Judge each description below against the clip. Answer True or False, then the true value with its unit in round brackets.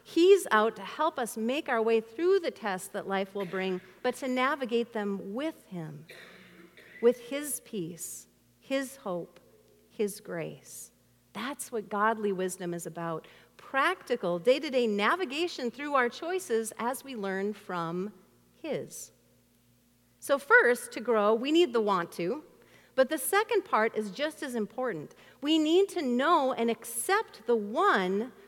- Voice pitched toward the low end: False (230 Hz)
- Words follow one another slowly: False (150 wpm)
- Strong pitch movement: True (6.3 semitones)